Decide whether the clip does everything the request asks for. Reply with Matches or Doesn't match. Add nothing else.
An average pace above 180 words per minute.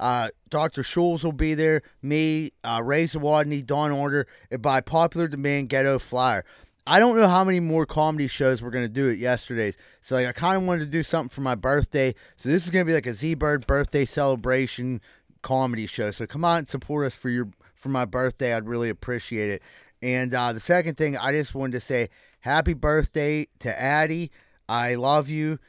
Matches